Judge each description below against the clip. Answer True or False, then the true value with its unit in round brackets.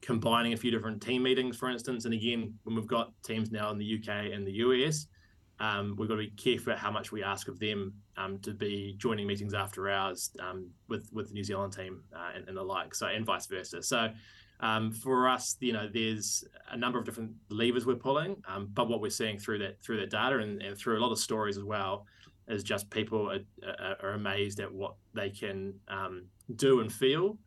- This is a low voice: True (110 Hz)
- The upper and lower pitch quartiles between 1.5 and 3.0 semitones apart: True (2.7 semitones)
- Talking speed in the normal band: False (225 wpm)